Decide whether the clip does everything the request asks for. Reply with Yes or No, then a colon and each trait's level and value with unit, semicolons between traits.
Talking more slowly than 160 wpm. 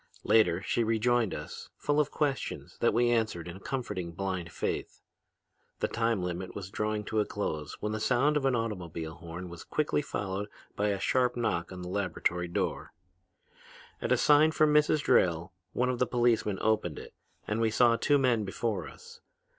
No: average, 185 wpm